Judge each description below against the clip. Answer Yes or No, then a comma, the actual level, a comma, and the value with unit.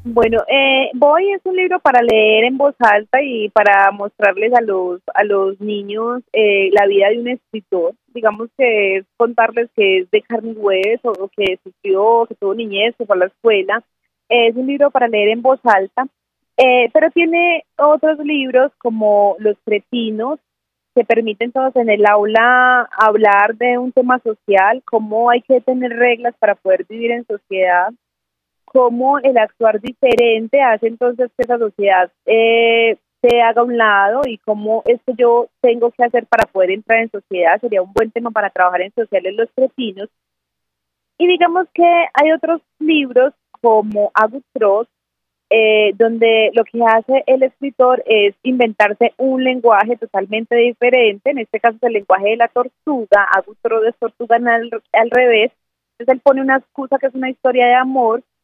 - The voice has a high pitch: Yes, high, 230 Hz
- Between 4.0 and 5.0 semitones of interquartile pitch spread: No, average, 3.3 semitones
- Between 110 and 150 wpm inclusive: No, average, 170 wpm